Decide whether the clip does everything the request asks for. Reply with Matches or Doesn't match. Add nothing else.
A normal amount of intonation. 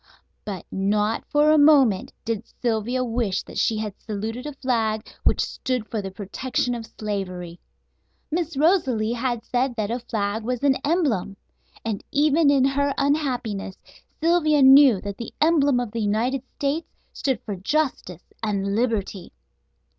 Matches